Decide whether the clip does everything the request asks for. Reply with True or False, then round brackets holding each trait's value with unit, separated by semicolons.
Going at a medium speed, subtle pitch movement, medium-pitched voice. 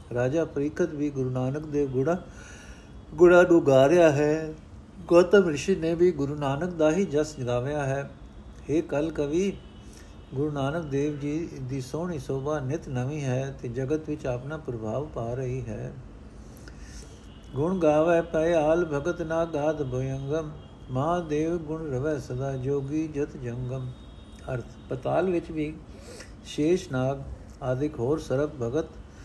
False (140 wpm; 3.5 semitones; 145 Hz)